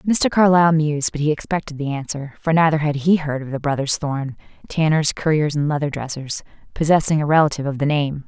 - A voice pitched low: No, medium, 150 Hz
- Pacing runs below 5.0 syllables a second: No, 6.0 syllables/s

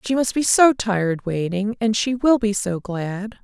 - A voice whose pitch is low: No, high, 215 Hz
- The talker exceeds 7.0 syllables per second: No, 4.3 syllables/s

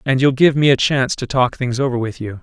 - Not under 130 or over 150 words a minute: No, fast, 295 wpm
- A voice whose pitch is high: No, low, 130 Hz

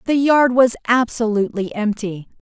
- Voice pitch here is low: No, high, 230 Hz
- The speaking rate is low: Yes, slow, 125 wpm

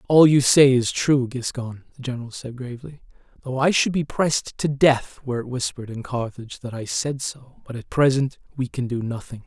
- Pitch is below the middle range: Yes, low, 130 Hz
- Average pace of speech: No, fast, 210 wpm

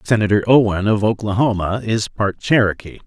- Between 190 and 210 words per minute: No, slow, 135 wpm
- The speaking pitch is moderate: No, low, 105 Hz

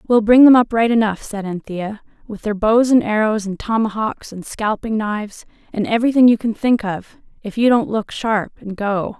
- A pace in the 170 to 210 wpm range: Yes, average, 200 wpm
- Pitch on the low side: No, high, 220 Hz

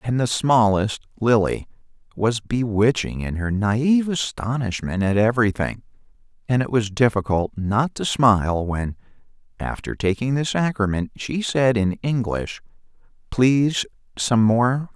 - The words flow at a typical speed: No, slow, 125 wpm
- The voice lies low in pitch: Yes, low, 115 Hz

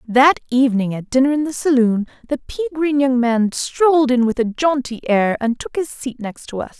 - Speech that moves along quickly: Yes, fast, 220 wpm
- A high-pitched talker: Yes, very high, 260 Hz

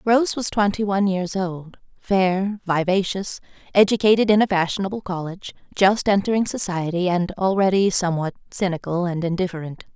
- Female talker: Yes, female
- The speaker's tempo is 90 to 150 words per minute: Yes, slow, 135 wpm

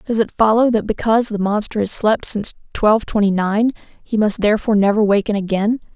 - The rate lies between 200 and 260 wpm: No, average, 190 wpm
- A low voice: No, high, 215 Hz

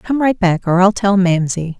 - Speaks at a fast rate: Yes, fast, 235 wpm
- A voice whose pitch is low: No, high, 190 Hz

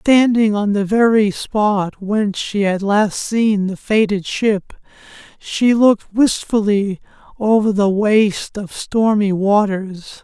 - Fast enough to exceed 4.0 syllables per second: No, 3.6 syllables/s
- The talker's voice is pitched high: Yes, high, 205 Hz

